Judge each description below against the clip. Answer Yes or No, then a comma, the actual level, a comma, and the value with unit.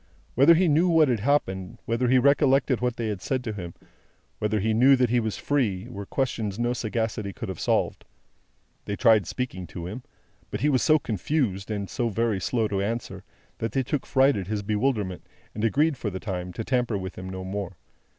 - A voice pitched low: Yes, low, 115 Hz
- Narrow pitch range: No, average, 4.5 semitones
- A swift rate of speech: Yes, fast, 210 wpm